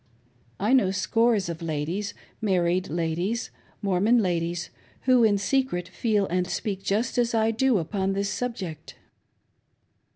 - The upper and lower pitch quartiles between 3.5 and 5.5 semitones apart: Yes, average, 4.4 semitones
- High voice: Yes, high, 195 Hz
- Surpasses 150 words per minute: No, slow, 135 wpm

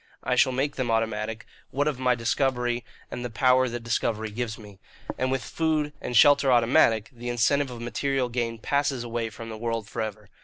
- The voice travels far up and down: No, narrow, 2.4 semitones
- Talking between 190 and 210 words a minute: Yes, average, 195 wpm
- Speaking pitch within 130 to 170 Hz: No, low, 120 Hz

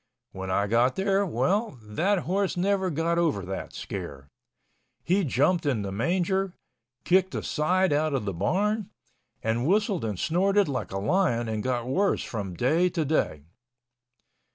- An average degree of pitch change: No, wide, 8.9 semitones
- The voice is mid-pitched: Yes, medium, 155 Hz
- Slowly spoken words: No, average, 155 wpm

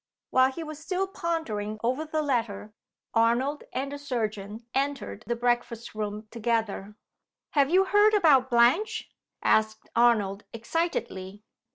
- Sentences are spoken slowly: Yes, slow, 130 wpm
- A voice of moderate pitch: No, high, 240 Hz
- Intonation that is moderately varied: No, wide, 5.8 semitones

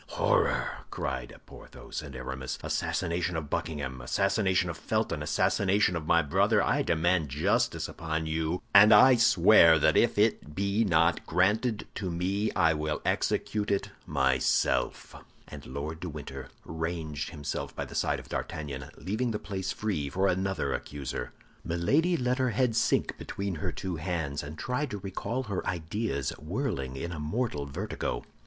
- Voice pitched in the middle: No, very low, 85 Hz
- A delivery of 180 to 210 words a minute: No, average, 155 wpm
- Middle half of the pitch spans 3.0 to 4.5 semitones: No, average, 5.1 semitones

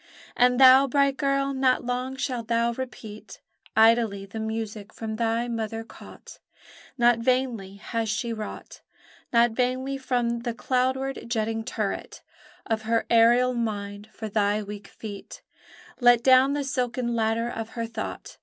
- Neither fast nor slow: Yes, average, 145 wpm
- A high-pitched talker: Yes, high, 235 Hz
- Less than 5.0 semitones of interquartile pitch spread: Yes, narrow, 2.4 semitones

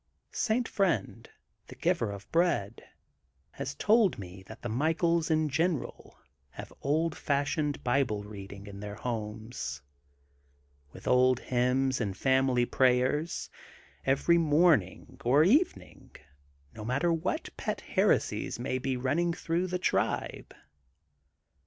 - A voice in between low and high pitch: No, low, 130 Hz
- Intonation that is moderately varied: No, wide, 6.5 semitones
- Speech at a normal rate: No, slow, 125 wpm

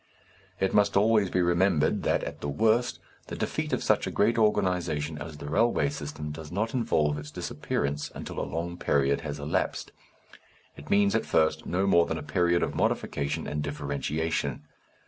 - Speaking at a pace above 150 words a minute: Yes, average, 175 wpm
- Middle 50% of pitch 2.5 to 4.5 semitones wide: No, average, 5.1 semitones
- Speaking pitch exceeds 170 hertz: No, very low, 80 Hz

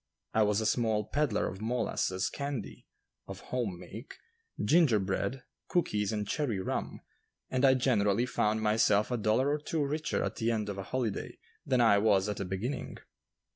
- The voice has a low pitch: Yes, low, 110 Hz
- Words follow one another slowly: No, average, 175 wpm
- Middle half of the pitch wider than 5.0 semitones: No, average, 3.8 semitones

